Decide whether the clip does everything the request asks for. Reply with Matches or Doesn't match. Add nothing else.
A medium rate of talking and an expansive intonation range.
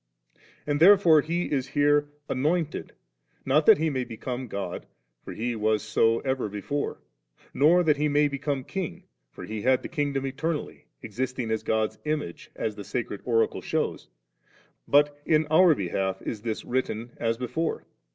Doesn't match